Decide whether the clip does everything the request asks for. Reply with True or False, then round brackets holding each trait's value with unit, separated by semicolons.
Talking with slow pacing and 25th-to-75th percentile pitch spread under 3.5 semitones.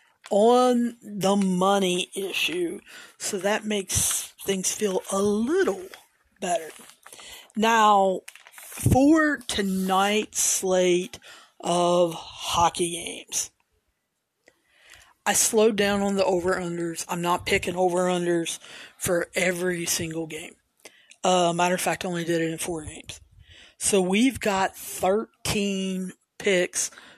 True (115 wpm; 2.8 semitones)